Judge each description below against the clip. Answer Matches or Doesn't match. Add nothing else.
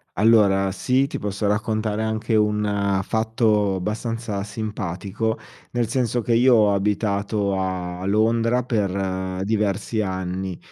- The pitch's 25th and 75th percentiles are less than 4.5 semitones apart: Matches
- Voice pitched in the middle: Doesn't match